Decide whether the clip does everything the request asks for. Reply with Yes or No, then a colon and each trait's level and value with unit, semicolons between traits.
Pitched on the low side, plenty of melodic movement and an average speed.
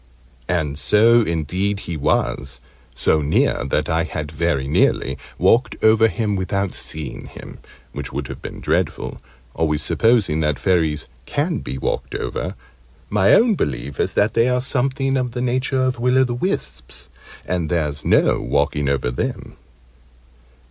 Yes: very low, 90 Hz; wide, 8.3 semitones; average, 155 wpm